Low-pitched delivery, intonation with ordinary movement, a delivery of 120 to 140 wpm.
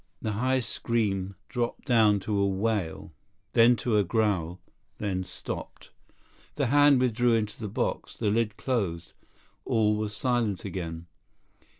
Yes: low, 110 Hz; average, 3.3 semitones; slow, 135 wpm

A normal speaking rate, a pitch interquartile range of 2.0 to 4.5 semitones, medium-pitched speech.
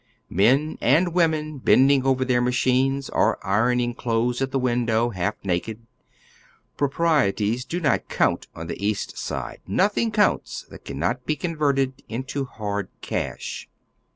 No: average, 145 wpm; average, 4.2 semitones; low, 130 Hz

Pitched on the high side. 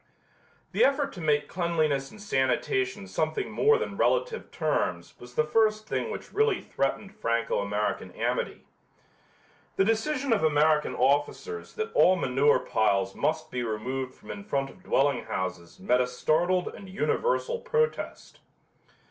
No: medium, 160 Hz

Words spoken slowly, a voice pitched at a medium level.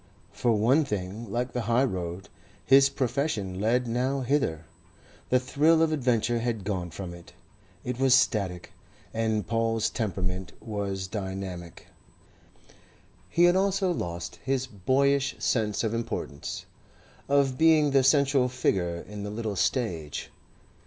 No: slow, 130 wpm; low, 115 Hz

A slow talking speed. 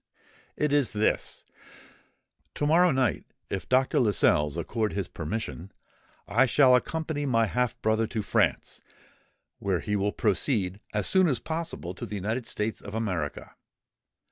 No: average, 145 wpm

